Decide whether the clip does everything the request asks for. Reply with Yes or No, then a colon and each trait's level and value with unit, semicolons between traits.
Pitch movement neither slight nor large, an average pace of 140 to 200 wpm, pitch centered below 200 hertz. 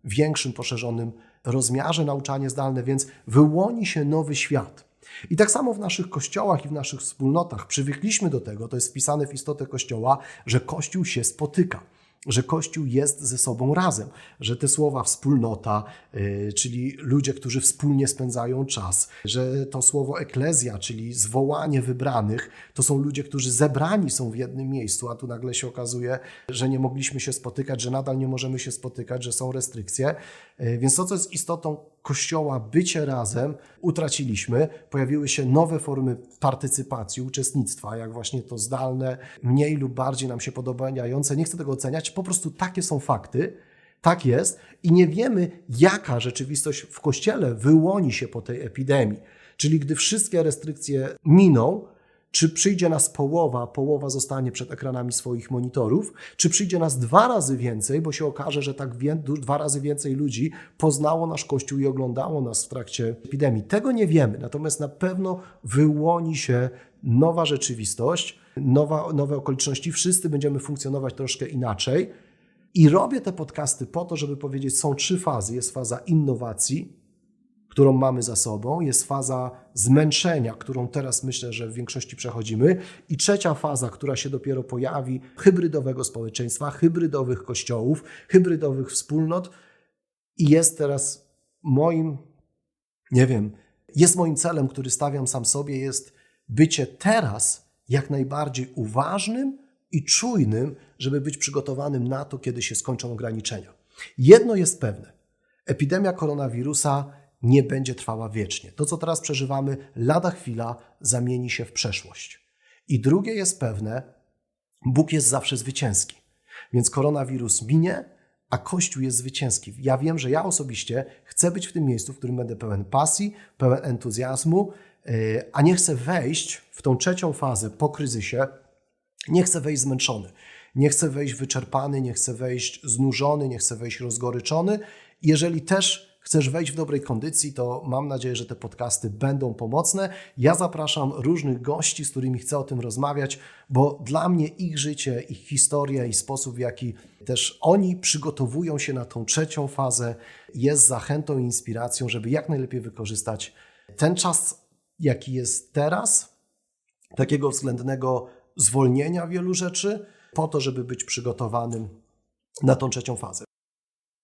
Yes: average, 3.6 semitones; average, 150 wpm; low, 135 Hz